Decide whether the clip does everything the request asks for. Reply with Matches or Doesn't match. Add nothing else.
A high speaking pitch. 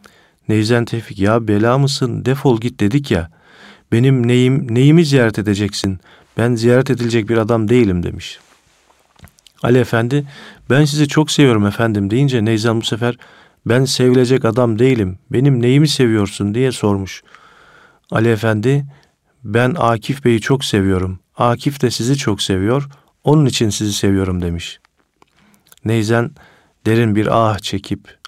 Doesn't match